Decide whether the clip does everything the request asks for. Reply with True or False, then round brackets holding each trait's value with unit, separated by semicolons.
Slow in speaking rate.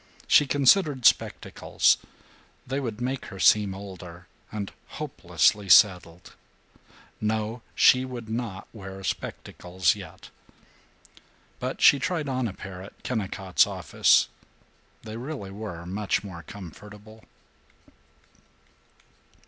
True (105 wpm)